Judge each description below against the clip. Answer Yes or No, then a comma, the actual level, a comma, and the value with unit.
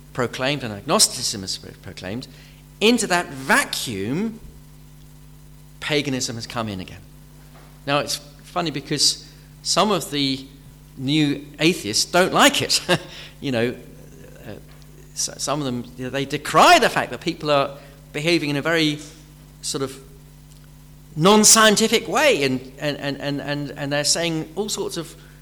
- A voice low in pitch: No, medium, 145 Hz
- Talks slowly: Yes, slow, 130 wpm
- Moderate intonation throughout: No, narrow, 1.8 semitones